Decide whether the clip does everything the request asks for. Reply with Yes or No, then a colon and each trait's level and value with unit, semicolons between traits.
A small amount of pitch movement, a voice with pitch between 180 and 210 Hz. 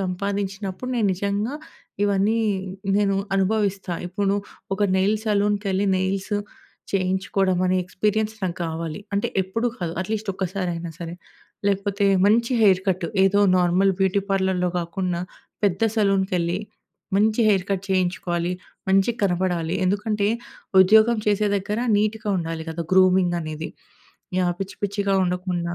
Yes: narrow, 2.0 semitones; high, 190 Hz